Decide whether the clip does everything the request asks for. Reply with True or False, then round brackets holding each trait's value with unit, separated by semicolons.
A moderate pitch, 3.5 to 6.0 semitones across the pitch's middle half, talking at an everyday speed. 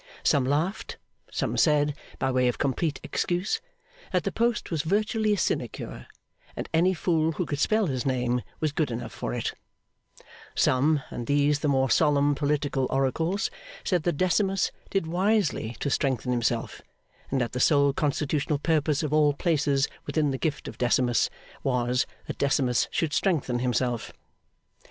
True (145 Hz; 3.8 semitones; 155 wpm)